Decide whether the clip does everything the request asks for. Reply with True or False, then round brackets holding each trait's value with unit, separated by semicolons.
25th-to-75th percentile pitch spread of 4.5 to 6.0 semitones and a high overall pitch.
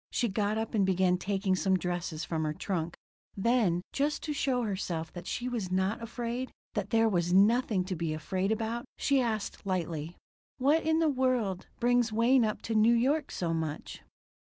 True (4.9 semitones; 210 Hz)